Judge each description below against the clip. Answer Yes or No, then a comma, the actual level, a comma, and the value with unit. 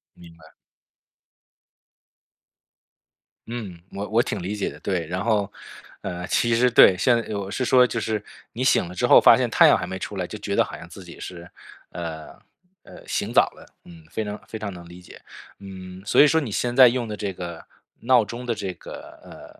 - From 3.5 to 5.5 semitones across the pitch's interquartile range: Yes, average, 4.5 semitones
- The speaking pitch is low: Yes, low, 100 Hz